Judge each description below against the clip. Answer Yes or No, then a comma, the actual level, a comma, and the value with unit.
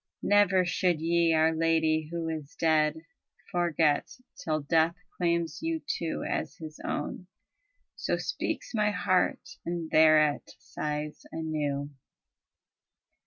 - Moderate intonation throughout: No, narrow, 1.8 semitones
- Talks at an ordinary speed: No, slow, 115 wpm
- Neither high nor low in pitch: Yes, medium, 160 Hz